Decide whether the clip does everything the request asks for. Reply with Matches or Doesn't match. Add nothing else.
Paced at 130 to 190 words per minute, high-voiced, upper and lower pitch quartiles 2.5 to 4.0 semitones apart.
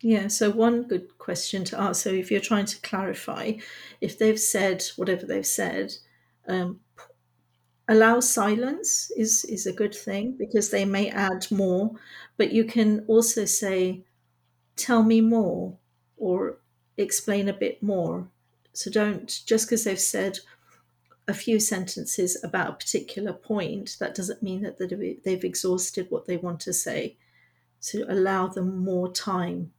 Matches